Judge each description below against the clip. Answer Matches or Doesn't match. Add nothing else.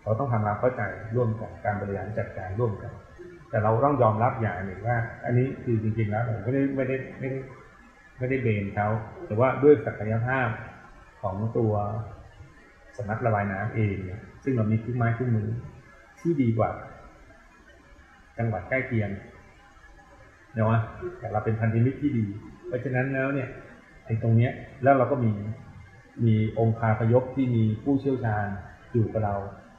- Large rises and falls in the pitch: Doesn't match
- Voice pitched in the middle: Doesn't match